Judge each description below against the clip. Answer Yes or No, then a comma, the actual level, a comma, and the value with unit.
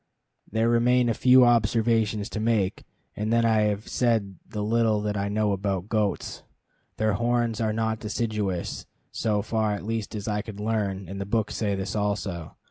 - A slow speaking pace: No, average, 180 wpm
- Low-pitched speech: Yes, low, 110 Hz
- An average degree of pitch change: No, narrow, 2.0 semitones